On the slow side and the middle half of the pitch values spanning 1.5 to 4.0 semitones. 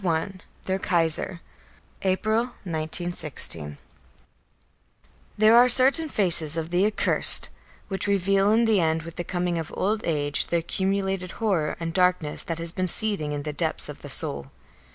No: average, 155 wpm; average, 3.7 semitones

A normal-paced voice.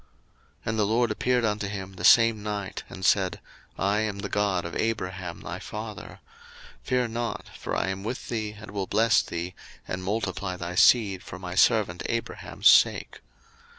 Yes: average, 175 wpm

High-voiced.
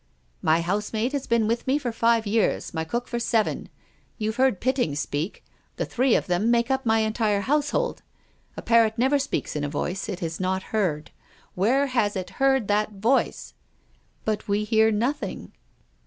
Yes: high, 220 Hz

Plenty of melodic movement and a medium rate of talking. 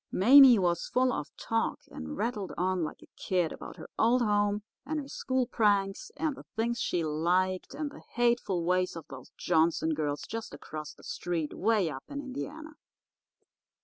Yes: wide, 6.6 semitones; average, 175 wpm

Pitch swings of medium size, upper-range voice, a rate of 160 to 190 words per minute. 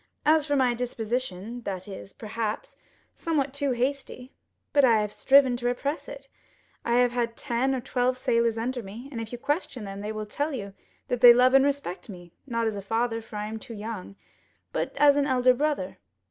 No: average, 3.6 semitones; high, 240 Hz; average, 200 wpm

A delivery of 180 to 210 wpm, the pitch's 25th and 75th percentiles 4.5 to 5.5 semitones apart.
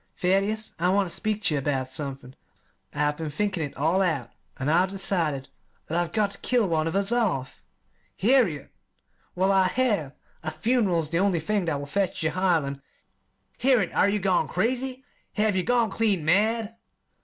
Yes: average, 185 wpm; average, 5.2 semitones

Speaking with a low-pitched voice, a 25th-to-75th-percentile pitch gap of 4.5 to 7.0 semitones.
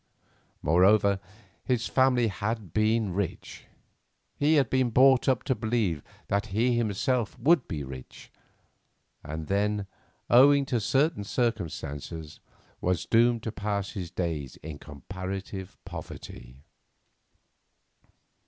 Yes: low, 105 Hz; wide, 5.4 semitones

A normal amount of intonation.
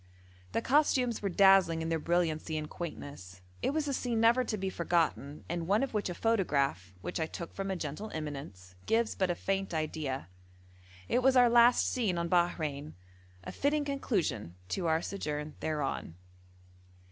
No: wide, 6.7 semitones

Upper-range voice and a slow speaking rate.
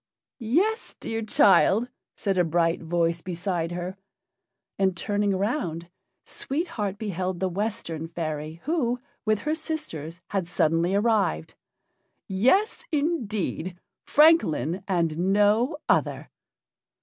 Yes: high, 195 Hz; slow, 110 wpm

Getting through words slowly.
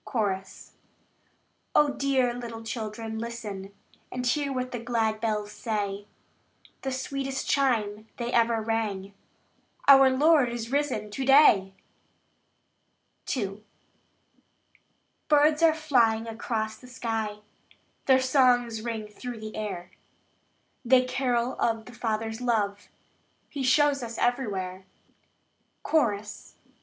Yes: slow, 110 wpm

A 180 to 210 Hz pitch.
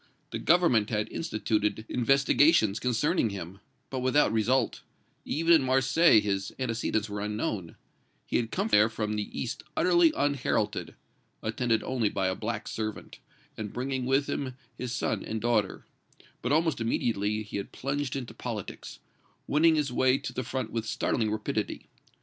No: low, 120 Hz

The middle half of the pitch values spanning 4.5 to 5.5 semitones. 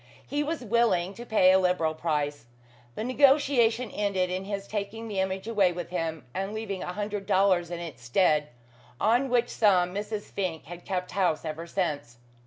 No: average, 4.0 semitones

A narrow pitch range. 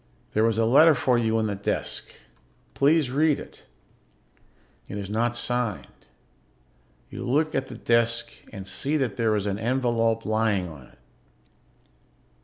No: average, 3.2 semitones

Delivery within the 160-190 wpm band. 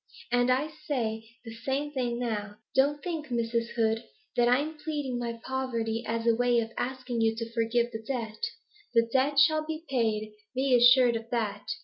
Yes: average, 175 wpm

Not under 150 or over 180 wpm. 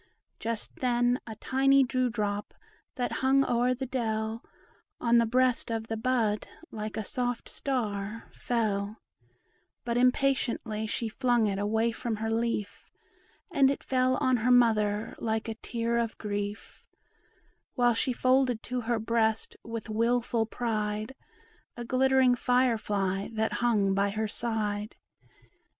No: average, 140 wpm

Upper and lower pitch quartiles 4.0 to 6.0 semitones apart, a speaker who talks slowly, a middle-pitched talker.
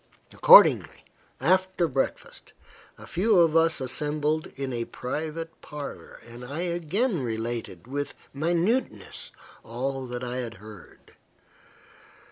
Yes: wide, 5.5 semitones; slow, 110 wpm; medium, 145 Hz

